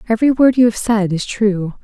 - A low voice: No, high, 220 Hz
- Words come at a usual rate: No, fast, 230 wpm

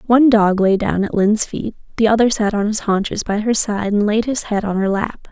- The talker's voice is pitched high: Yes, high, 210 Hz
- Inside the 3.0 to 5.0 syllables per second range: No, 5.5 syllables/s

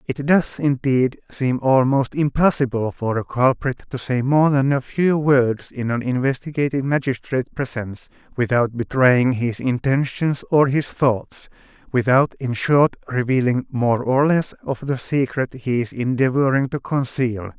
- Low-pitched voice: Yes, low, 130 Hz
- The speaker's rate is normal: Yes, average, 145 wpm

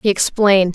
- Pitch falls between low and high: No, high, 195 Hz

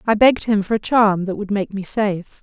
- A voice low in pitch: No, high, 205 Hz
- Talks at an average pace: No, fast, 270 wpm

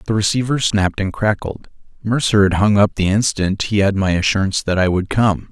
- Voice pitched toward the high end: No, low, 100 Hz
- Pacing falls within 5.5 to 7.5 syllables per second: Yes, 5.6 syllables/s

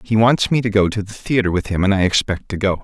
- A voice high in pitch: No, low, 100 Hz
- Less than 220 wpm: No, fast, 315 wpm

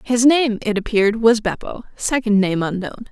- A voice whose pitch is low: No, high, 220 Hz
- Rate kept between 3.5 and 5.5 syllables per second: Yes, 5.0 syllables/s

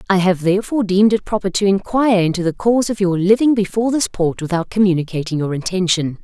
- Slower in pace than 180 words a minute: No, average, 200 wpm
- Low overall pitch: No, high, 195 Hz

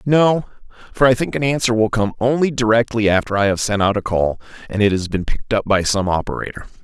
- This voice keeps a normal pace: No, fast, 230 wpm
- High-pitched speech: No, low, 115 Hz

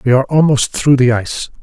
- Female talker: No, male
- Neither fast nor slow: No, fast, 220 wpm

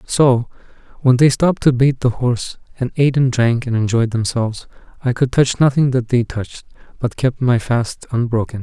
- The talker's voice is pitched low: Yes, low, 125 Hz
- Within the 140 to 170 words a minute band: No, average, 190 wpm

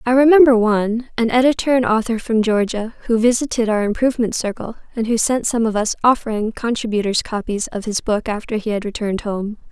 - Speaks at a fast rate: No, average, 190 wpm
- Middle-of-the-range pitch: No, high, 225 Hz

